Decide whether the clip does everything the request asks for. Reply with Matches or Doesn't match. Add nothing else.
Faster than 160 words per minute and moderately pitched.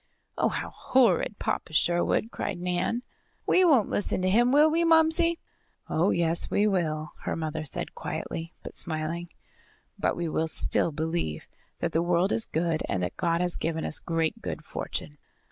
Matches